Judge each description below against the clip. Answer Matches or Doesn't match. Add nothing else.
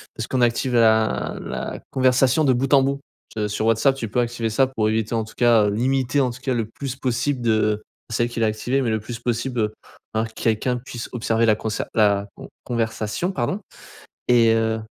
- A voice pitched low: Matches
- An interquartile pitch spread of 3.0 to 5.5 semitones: Doesn't match